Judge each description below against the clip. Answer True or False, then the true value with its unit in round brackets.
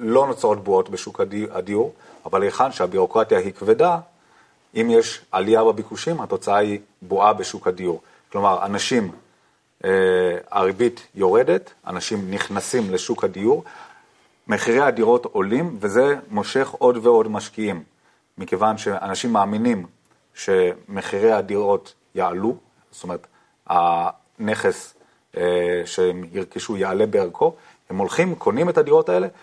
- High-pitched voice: True (240 Hz)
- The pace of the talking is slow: False (115 wpm)